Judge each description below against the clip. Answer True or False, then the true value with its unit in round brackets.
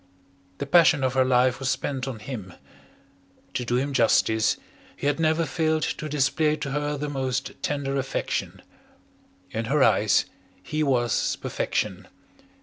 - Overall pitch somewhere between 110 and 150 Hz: True (135 Hz)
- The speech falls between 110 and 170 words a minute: True (145 wpm)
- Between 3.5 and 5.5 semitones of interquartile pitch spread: False (2.8 semitones)